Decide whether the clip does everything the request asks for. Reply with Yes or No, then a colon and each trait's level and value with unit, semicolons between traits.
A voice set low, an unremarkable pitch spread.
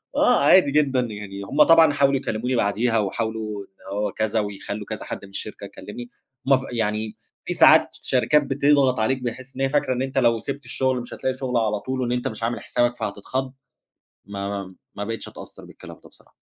Yes: low, 120 Hz; average, 3.9 semitones